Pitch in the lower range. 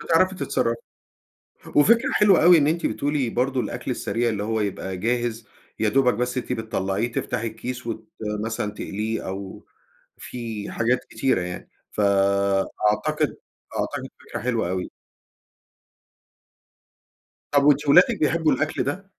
Yes: low, 115 Hz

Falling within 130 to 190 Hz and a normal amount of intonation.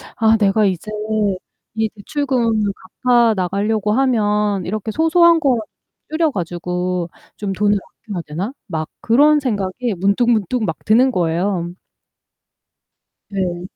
No: high, 210 Hz; average, 4.6 semitones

